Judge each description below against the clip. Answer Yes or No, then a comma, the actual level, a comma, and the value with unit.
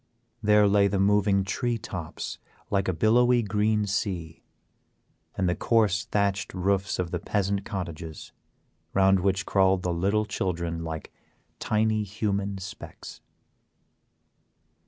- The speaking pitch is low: Yes, low, 100 Hz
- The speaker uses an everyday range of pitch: No, narrow, 2.3 semitones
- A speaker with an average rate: No, slow, 120 wpm